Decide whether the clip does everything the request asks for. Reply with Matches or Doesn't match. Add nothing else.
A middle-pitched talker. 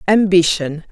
Matches